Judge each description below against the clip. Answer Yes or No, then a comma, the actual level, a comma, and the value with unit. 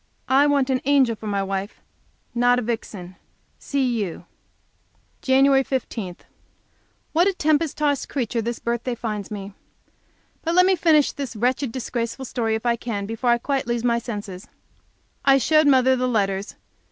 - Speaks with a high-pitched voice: Yes, high, 245 Hz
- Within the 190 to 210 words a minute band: No, average, 165 wpm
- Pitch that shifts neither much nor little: Yes, average, 3.8 semitones